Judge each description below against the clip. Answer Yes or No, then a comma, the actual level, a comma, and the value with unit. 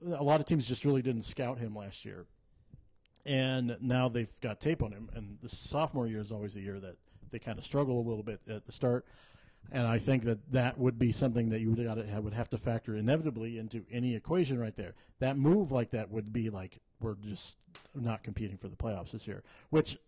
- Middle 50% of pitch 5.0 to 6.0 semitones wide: No, average, 3.2 semitones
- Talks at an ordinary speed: No, fast, 220 wpm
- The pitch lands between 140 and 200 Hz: No, low, 115 Hz